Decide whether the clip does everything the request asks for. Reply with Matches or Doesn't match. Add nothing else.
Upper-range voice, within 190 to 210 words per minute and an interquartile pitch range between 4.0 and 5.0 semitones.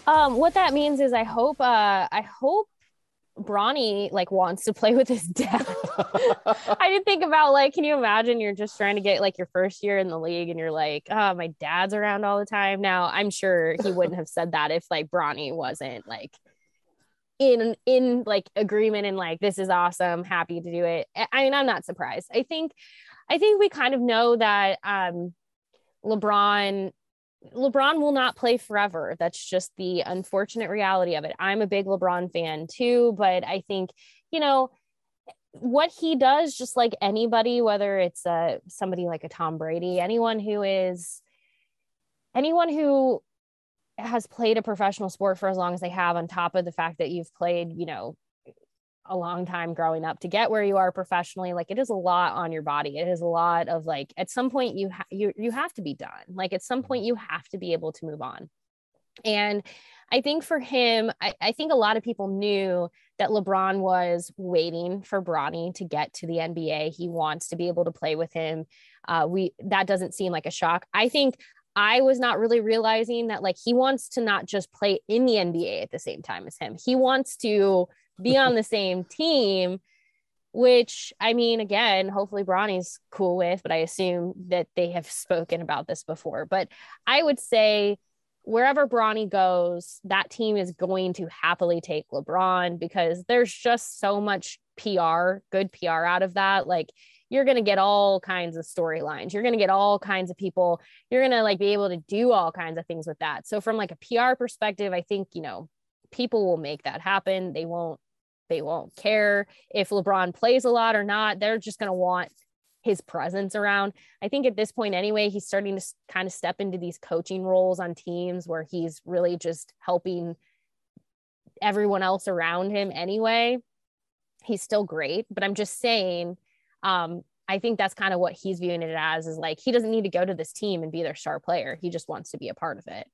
Matches